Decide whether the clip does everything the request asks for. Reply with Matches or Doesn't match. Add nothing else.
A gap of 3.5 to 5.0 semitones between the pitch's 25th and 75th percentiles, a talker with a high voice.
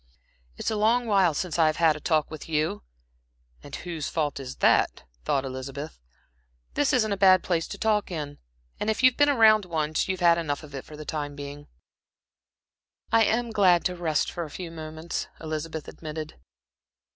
Doesn't match